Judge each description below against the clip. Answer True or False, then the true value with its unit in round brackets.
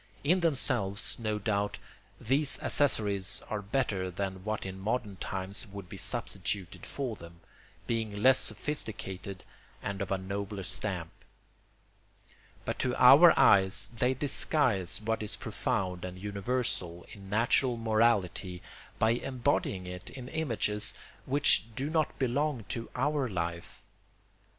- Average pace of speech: False (125 wpm)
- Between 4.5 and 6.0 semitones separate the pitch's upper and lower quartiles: True (4.8 semitones)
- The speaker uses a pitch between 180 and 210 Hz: False (105 Hz)